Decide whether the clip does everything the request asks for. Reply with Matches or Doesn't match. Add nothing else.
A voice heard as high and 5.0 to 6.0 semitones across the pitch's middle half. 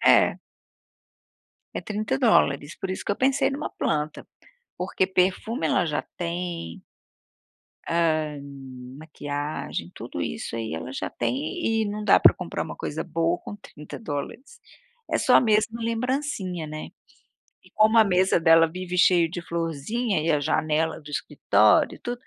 Doesn't match